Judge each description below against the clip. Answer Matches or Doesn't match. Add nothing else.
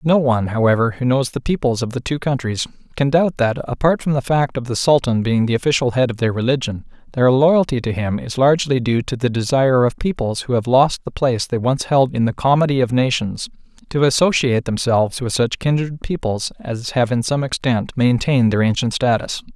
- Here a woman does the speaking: Doesn't match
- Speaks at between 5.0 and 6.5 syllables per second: Matches